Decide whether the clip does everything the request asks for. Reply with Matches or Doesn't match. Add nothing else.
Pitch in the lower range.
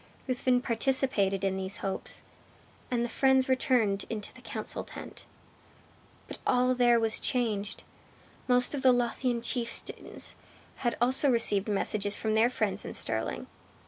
Doesn't match